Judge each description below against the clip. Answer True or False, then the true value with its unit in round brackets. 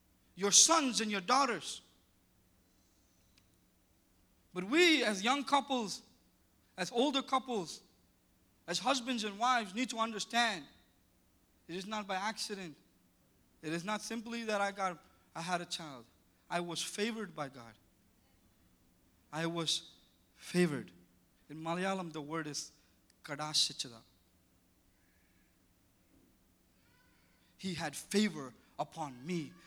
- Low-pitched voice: False (165 Hz)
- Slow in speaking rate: True (110 wpm)